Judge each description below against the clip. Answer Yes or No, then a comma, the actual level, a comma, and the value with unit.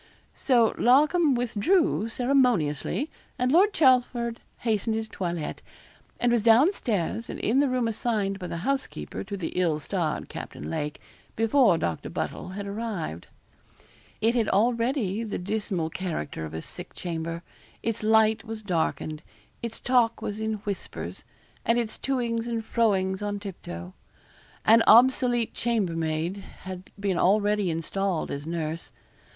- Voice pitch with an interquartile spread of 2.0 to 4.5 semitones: No, average, 5.0 semitones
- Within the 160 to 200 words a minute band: No, average, 145 wpm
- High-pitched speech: Yes, high, 215 Hz